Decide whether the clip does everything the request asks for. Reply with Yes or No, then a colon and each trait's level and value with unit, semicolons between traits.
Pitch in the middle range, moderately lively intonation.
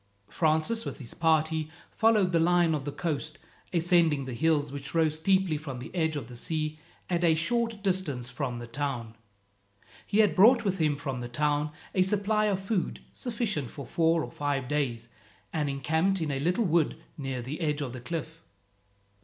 Yes: medium, 155 Hz; average, 4.1 semitones